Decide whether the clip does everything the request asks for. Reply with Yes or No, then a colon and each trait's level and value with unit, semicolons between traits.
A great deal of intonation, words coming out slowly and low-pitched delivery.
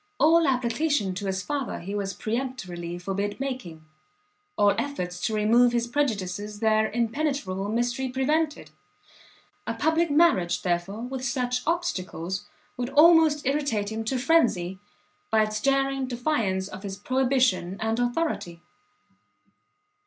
No: wide, 5.7 semitones; slow, 125 wpm; high, 235 Hz